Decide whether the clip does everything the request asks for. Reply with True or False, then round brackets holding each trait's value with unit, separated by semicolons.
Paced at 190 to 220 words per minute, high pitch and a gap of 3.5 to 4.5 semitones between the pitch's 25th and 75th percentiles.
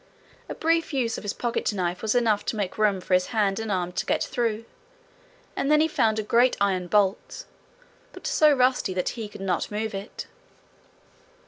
True (195 wpm; 215 Hz; 3.8 semitones)